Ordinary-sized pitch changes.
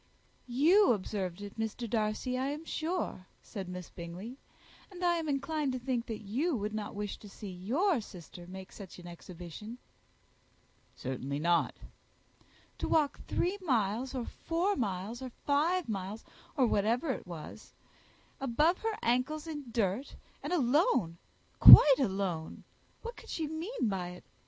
No: wide, 7.6 semitones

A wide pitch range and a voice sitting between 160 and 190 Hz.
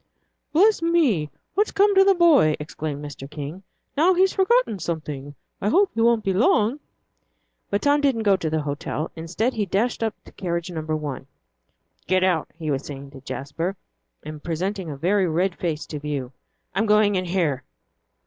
Yes: wide, 7.1 semitones; medium, 185 Hz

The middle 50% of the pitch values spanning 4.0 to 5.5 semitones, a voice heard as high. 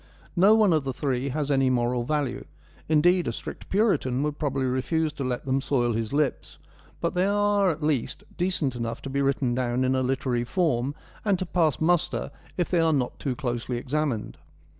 No: average, 4.5 semitones; medium, 140 Hz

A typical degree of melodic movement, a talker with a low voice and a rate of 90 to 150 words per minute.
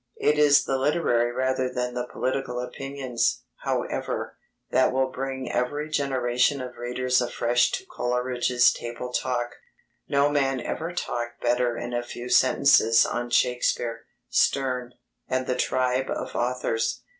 No: narrow, 1.6 semitones; low, 125 Hz; slow, 135 wpm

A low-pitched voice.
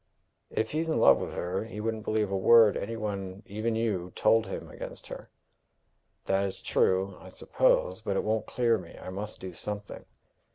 Yes: low, 105 Hz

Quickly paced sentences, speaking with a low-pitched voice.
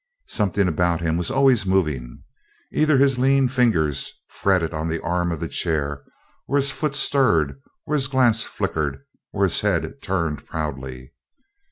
No: average, 155 wpm; very low, 90 Hz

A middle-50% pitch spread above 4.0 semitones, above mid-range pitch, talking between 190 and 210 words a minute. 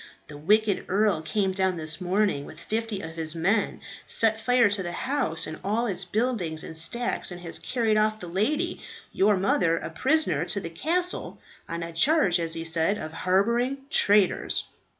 No: average, 5.1 semitones; high, 195 Hz; average, 180 wpm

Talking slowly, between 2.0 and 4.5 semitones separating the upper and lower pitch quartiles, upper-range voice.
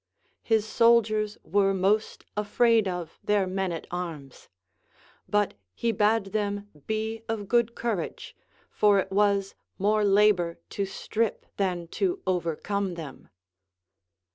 Yes: slow, 125 wpm; narrow, 2.4 semitones; high, 205 Hz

